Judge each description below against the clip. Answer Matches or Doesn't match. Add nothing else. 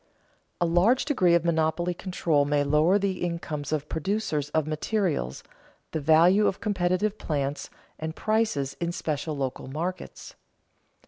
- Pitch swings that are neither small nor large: Matches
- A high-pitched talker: Doesn't match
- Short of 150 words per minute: Matches